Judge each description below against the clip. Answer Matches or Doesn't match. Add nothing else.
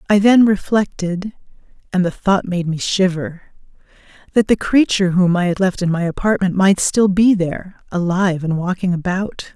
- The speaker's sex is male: Doesn't match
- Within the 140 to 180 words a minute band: Matches